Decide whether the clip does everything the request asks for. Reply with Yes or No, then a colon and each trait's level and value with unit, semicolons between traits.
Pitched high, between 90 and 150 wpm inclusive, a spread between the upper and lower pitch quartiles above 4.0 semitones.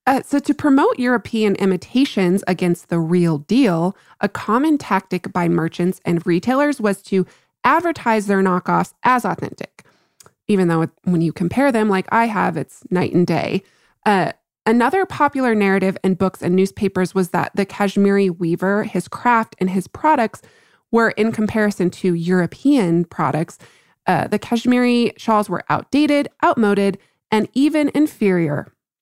Yes: high, 200 Hz; average, 145 wpm; average, 4.7 semitones